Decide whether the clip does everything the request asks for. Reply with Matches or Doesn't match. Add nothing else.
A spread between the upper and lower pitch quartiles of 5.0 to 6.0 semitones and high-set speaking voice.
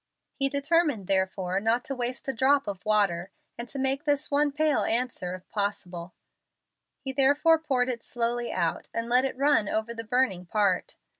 Matches